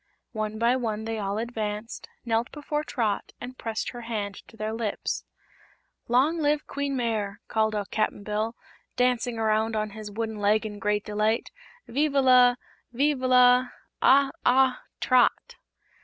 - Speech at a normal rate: Yes, average, 150 wpm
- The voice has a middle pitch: No, high, 230 Hz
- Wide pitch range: No, average, 2.9 semitones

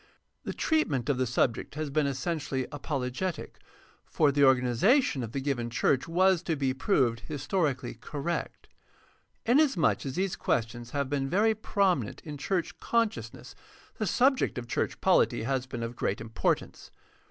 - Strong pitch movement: Yes, wide, 6.3 semitones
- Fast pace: No, average, 155 wpm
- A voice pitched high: No, medium, 140 Hz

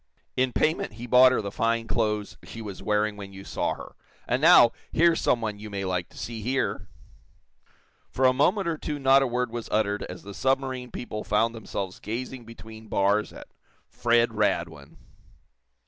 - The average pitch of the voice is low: Yes, low, 115 Hz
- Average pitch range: Yes, average, 3.5 semitones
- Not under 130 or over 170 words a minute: No, average, 180 wpm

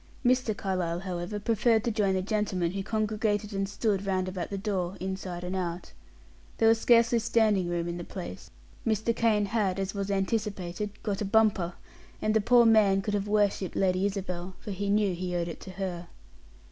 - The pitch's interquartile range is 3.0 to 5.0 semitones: No, narrow, 2.6 semitones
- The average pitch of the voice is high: Yes, high, 195 Hz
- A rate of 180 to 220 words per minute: Yes, average, 190 wpm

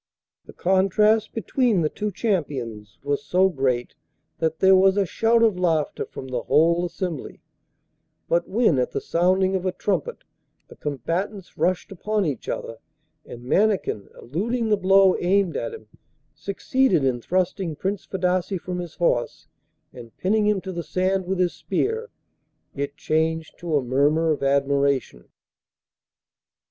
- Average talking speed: Yes, average, 150 wpm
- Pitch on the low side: No, medium, 180 Hz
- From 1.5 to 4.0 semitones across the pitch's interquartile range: No, average, 5.1 semitones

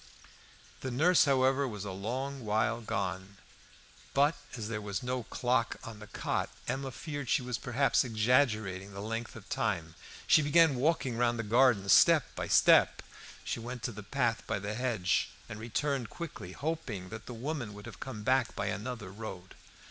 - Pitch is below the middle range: Yes, low, 115 Hz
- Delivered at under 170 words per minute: No, average, 175 wpm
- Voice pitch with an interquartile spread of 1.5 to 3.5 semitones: No, average, 3.9 semitones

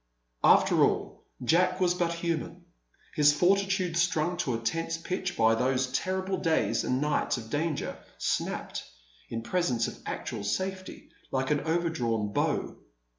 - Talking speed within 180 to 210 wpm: No, average, 140 wpm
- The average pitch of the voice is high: No, medium, 165 Hz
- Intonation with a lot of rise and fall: Yes, wide, 5.9 semitones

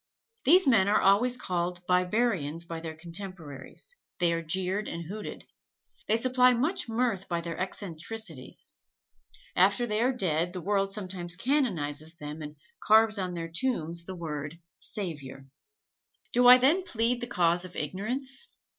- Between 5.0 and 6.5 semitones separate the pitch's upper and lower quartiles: Yes, wide, 5.6 semitones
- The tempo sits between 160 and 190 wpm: No, average, 145 wpm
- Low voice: No, medium, 185 Hz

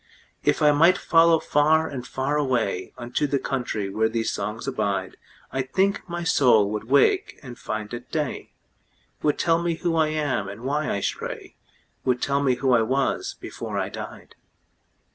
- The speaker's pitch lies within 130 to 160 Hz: Yes, low, 135 Hz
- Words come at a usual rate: Yes, average, 160 wpm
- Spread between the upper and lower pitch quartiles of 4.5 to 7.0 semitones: Yes, average, 5.2 semitones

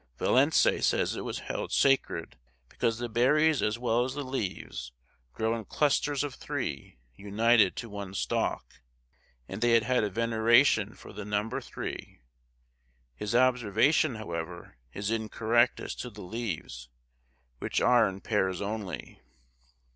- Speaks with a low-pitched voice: Yes, low, 115 Hz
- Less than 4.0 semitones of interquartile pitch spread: Yes, average, 3.4 semitones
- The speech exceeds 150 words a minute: No, average, 140 wpm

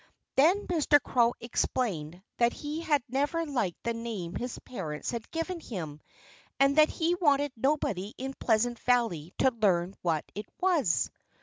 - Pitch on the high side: Yes, high, 245 Hz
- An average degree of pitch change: No, wide, 6.8 semitones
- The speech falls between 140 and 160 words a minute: Yes, average, 150 wpm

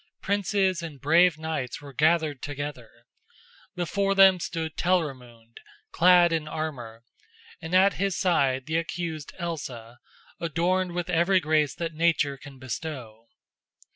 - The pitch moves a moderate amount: Yes, average, 4.1 semitones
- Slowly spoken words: Yes, slow, 125 wpm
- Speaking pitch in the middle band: Yes, medium, 160 Hz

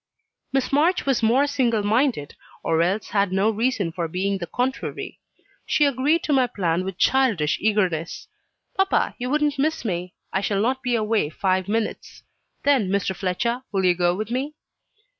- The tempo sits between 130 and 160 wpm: No, average, 170 wpm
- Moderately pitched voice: No, high, 215 Hz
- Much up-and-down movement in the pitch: Yes, wide, 6.0 semitones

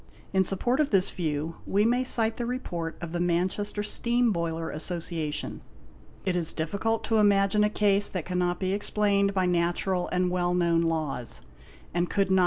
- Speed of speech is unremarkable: Yes, average, 175 wpm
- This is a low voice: No, medium, 185 Hz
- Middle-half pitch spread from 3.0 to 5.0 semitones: Yes, average, 3.3 semitones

